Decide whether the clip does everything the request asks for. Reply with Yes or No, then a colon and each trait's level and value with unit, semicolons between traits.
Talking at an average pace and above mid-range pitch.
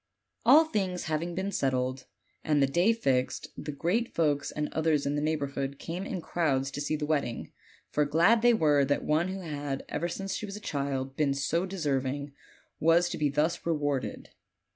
No: average, 185 wpm; medium, 150 Hz